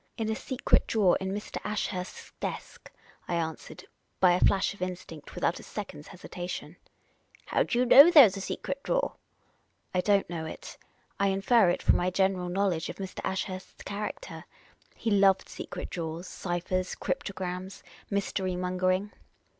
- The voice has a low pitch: No, high, 190 Hz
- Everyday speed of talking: Yes, average, 170 wpm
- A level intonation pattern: Yes, narrow, 2.1 semitones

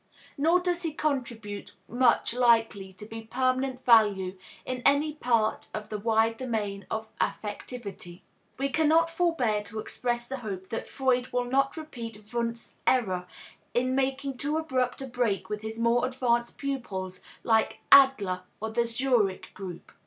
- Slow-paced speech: No, average, 155 wpm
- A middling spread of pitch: Yes, average, 3.7 semitones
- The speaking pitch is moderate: No, high, 240 Hz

